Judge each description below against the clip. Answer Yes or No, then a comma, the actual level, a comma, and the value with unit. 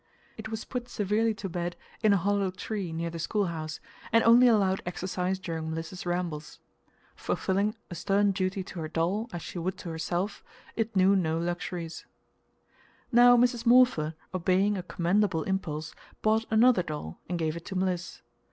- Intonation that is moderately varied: Yes, average, 3.9 semitones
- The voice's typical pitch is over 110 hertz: Yes, medium, 185 Hz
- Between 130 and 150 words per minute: No, average, 165 wpm